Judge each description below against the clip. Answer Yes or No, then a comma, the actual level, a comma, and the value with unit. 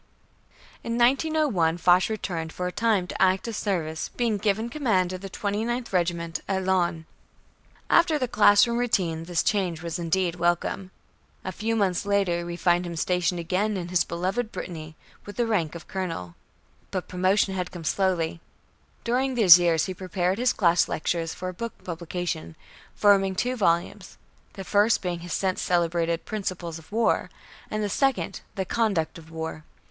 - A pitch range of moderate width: Yes, average, 3.6 semitones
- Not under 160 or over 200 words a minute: Yes, average, 165 wpm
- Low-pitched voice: No, medium, 185 Hz